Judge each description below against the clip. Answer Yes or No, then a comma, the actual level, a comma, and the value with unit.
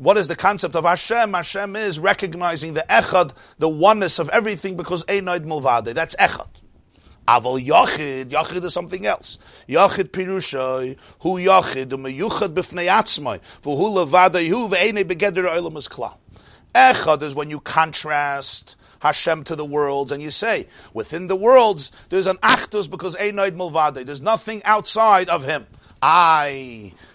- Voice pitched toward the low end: No, medium, 170 Hz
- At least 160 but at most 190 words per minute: No, average, 145 wpm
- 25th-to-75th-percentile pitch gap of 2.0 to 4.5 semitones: No, average, 4.9 semitones